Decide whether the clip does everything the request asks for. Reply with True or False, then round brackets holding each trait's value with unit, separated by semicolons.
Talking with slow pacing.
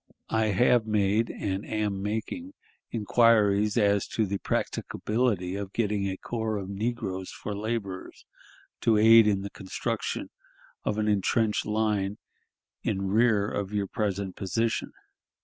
True (130 wpm)